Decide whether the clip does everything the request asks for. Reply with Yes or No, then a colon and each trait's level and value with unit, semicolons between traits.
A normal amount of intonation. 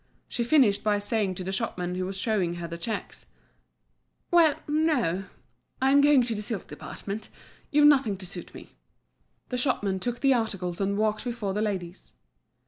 Yes: average, 4.7 semitones